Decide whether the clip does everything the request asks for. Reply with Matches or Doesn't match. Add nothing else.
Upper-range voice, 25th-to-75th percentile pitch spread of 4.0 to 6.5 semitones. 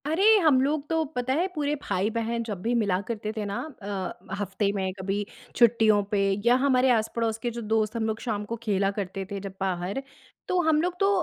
Matches